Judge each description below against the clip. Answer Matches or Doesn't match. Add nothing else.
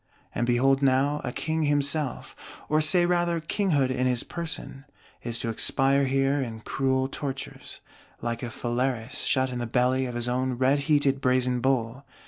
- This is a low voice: Matches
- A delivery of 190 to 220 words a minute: Doesn't match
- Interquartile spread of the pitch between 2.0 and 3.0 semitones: Matches